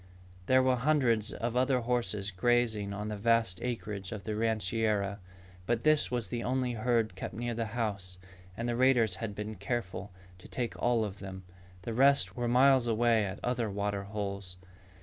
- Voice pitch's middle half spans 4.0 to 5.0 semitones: No, average, 3.2 semitones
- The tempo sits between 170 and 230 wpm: Yes, average, 175 wpm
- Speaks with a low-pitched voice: Yes, low, 115 Hz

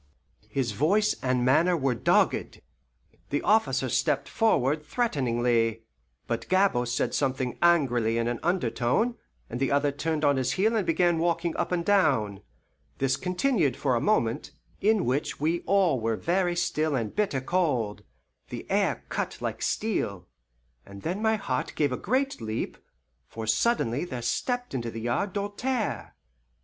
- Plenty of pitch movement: Yes, wide, 7.6 semitones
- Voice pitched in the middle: Yes, medium, 145 Hz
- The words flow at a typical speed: Yes, average, 155 wpm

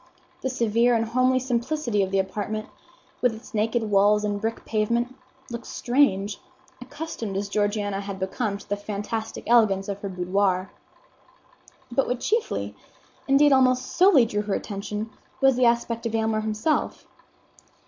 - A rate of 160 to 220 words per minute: No, average, 150 wpm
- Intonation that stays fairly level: No, average, 3.4 semitones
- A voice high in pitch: Yes, high, 220 Hz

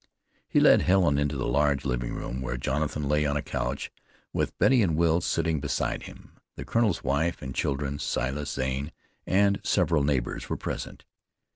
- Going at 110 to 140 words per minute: No, average, 170 wpm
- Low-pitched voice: Yes, very low, 70 Hz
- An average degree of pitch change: Yes, average, 3.4 semitones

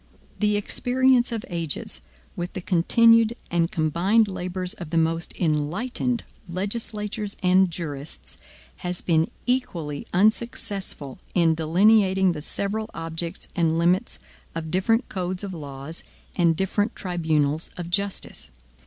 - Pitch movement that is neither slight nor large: Yes, average, 4.1 semitones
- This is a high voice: No, medium, 180 Hz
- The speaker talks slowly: Yes, slow, 120 wpm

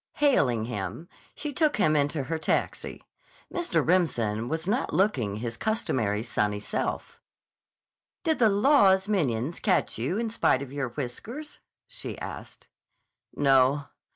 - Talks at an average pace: No, slow, 130 wpm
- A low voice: No, medium, 145 Hz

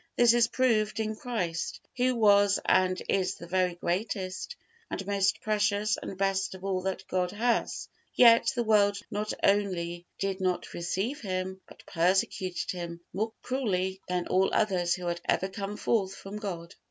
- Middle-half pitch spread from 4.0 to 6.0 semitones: No, narrow, 2.6 semitones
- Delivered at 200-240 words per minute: No, average, 165 wpm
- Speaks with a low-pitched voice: No, high, 195 Hz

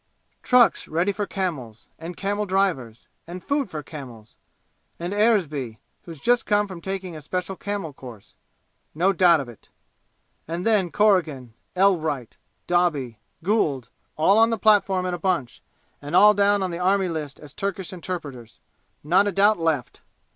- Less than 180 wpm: Yes, average, 160 wpm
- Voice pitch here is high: No, medium, 180 Hz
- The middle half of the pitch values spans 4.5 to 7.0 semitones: Yes, average, 5.0 semitones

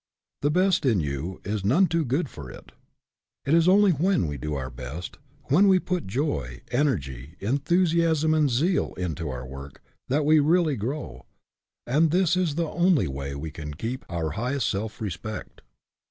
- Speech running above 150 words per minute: Yes, average, 170 wpm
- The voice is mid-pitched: No, low, 130 Hz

